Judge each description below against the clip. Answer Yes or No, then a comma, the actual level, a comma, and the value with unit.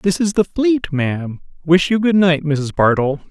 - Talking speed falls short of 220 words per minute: Yes, average, 200 wpm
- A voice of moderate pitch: Yes, medium, 160 Hz